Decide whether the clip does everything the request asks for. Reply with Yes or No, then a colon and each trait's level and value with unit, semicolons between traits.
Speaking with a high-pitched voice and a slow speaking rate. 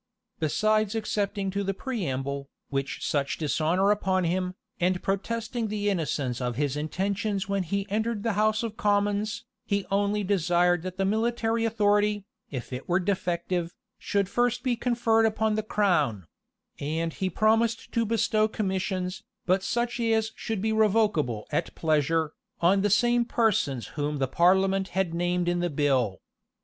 No: high, 195 Hz; average, 155 wpm